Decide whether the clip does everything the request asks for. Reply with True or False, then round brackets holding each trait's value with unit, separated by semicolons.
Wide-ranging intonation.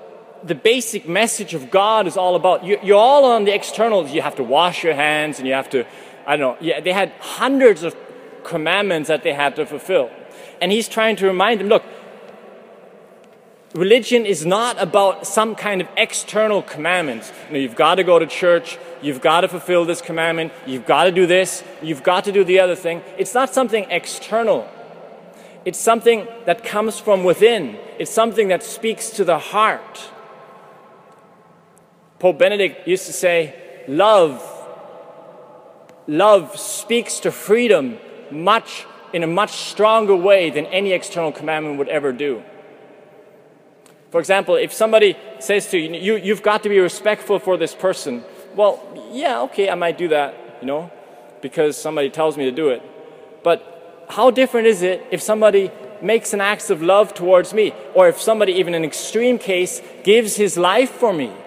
False (4.3 semitones)